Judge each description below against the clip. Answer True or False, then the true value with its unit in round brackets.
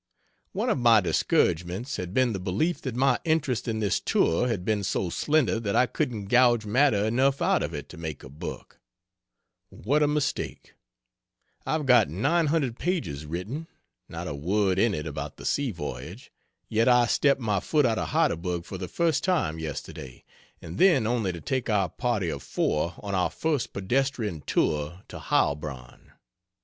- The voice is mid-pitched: False (110 Hz)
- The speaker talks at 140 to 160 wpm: False (175 wpm)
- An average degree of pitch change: False (7.2 semitones)